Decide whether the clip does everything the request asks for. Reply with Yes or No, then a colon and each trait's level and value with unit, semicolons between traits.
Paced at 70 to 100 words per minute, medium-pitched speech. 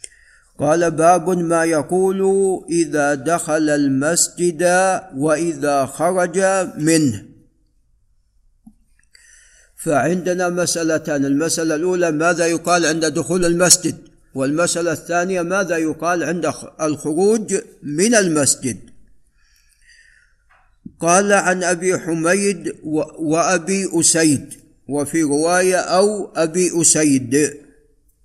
Yes: average, 80 wpm; medium, 165 Hz